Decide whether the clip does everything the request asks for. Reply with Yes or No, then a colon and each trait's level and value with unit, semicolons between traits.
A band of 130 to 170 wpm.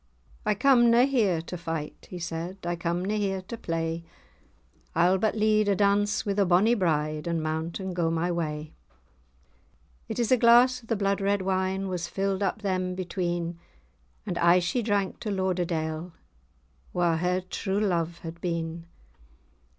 Yes: average, 165 wpm